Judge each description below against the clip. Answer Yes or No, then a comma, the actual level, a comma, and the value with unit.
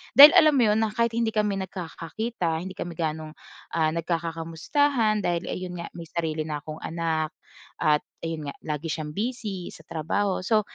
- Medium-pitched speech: Yes, medium, 170 Hz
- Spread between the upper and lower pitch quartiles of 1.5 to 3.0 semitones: No, average, 5.0 semitones